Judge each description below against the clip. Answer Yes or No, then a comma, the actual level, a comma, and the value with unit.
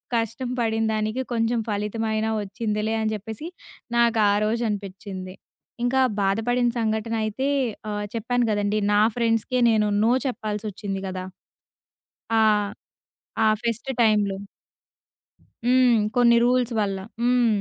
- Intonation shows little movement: Yes, narrow, 2.3 semitones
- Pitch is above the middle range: Yes, high, 220 Hz